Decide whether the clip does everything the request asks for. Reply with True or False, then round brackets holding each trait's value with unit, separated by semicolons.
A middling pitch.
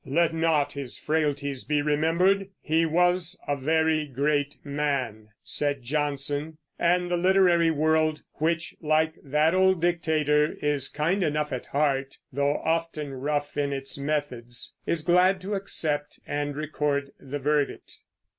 True (150 Hz)